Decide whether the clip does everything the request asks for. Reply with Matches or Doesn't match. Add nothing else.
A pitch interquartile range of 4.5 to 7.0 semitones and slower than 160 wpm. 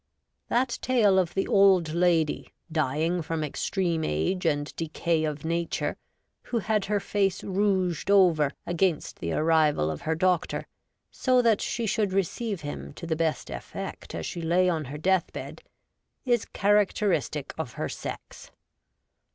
Doesn't match